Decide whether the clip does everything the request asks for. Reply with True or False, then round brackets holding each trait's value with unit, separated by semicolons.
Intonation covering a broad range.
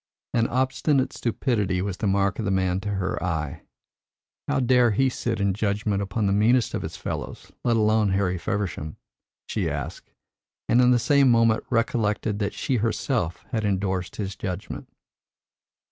False (3.4 semitones)